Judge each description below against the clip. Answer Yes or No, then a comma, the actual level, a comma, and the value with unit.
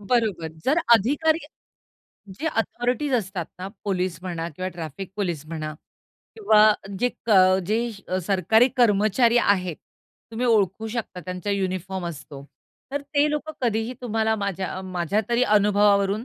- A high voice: Yes, high, 205 Hz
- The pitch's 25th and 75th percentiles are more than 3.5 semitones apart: Yes, average, 4.3 semitones